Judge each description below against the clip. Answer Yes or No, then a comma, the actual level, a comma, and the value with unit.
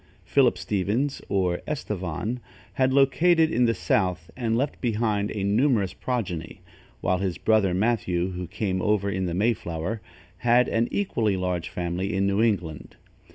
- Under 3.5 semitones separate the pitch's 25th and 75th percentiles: No, average, 4.4 semitones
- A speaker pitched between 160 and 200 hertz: No, low, 105 Hz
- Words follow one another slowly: No, average, 155 wpm